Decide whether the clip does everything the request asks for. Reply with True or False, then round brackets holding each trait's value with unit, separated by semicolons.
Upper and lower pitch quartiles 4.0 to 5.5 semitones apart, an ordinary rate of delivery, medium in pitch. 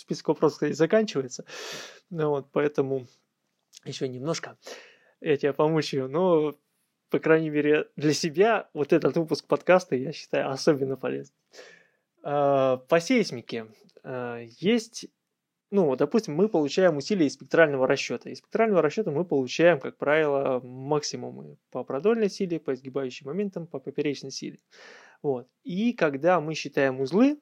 True (4.3 semitones; 135 wpm; 150 Hz)